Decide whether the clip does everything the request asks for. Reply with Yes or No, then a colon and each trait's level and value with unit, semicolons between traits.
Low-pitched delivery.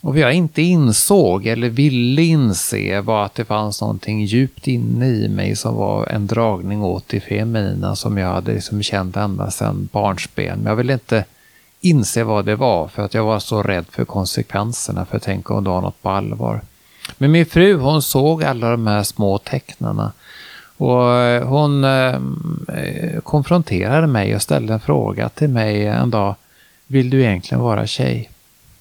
Yes: low, 110 Hz